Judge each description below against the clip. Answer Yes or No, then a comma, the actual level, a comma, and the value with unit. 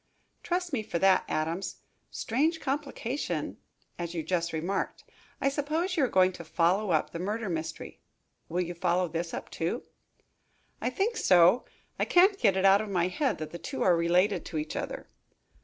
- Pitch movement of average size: No, wide, 7.7 semitones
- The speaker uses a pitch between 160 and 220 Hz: Yes, medium, 185 Hz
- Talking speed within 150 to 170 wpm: No, average, 180 wpm